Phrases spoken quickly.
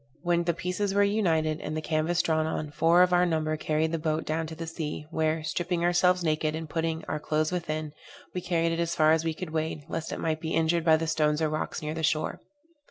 Yes: fast, 240 wpm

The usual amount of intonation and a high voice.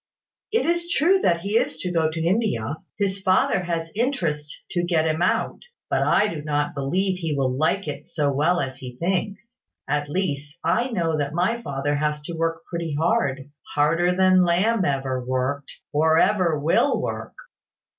No: average, 4.4 semitones; medium, 165 Hz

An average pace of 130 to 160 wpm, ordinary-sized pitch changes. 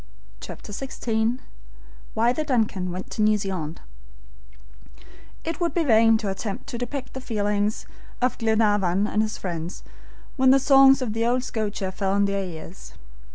Yes: average, 155 wpm; average, 4.1 semitones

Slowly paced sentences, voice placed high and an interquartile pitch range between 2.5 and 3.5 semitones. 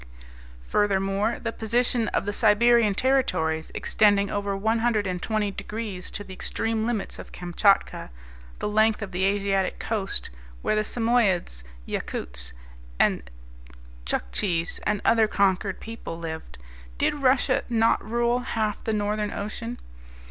Yes: slow, 125 wpm; high, 210 Hz; average, 2.8 semitones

